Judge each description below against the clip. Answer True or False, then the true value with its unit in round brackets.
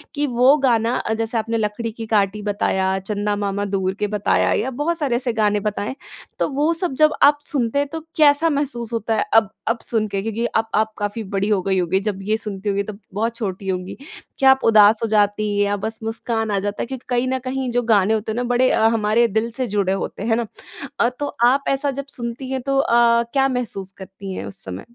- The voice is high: True (225 Hz)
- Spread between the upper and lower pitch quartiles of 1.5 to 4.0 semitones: True (3.3 semitones)